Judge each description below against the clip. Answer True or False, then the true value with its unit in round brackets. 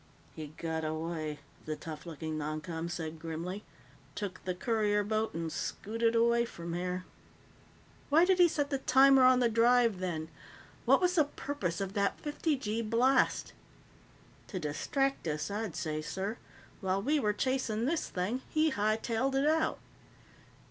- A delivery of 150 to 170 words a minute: True (155 wpm)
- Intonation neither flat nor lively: False (7.4 semitones)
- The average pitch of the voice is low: False (210 Hz)